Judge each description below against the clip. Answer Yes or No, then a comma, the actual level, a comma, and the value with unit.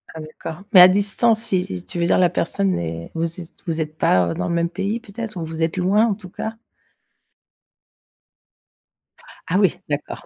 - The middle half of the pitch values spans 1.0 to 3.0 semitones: No, average, 3.7 semitones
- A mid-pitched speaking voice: Yes, medium, 180 Hz